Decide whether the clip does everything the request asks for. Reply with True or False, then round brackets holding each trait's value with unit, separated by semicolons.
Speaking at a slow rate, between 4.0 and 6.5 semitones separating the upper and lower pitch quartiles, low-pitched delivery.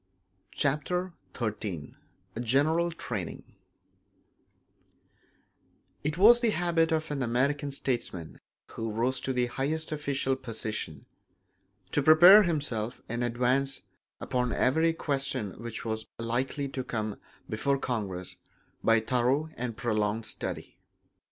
True (110 wpm; 4.8 semitones; 130 Hz)